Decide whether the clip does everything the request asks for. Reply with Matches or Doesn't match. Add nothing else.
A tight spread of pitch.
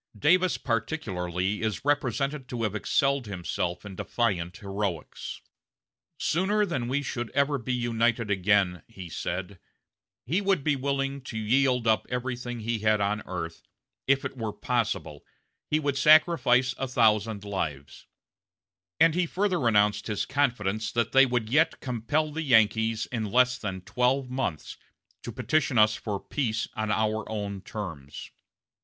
Doesn't match